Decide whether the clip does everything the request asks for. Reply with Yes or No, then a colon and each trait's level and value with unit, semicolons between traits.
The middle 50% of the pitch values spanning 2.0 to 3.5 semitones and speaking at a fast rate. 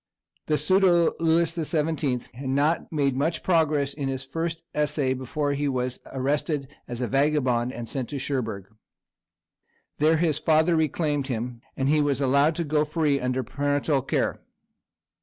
No: average, 3.0 semitones; average, 160 wpm